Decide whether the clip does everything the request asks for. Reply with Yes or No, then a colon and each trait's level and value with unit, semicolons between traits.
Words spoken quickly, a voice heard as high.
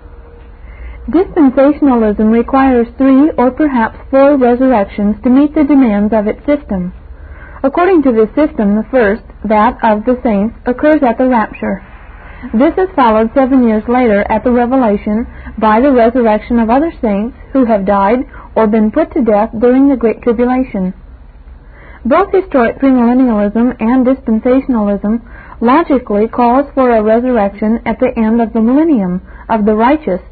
No: average, 145 wpm; high, 235 Hz